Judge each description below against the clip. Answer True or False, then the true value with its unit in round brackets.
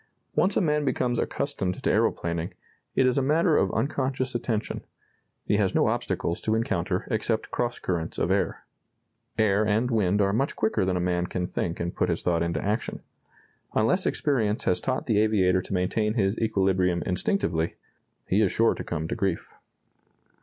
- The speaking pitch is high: False (105 Hz)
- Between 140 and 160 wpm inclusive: False (175 wpm)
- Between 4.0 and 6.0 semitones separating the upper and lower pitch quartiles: True (4.9 semitones)